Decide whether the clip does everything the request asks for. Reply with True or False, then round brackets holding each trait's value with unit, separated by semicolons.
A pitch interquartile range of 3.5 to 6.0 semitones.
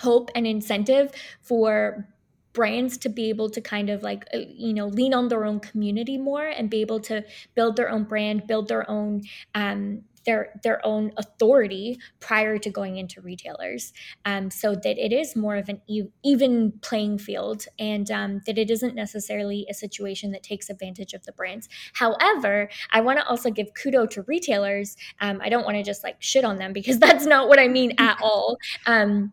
False (2.8 semitones)